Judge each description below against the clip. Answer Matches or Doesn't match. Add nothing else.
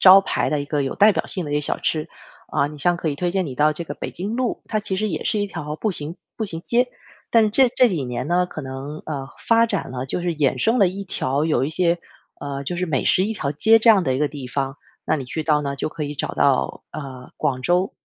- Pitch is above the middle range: Doesn't match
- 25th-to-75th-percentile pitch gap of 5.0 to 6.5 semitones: Matches